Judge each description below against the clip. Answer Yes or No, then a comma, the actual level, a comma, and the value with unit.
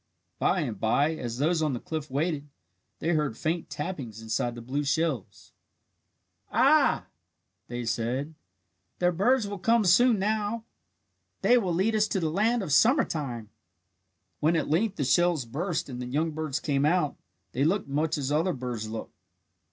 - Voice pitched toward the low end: No, medium, 155 Hz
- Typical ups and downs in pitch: No, wide, 5.9 semitones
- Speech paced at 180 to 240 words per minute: No, average, 165 wpm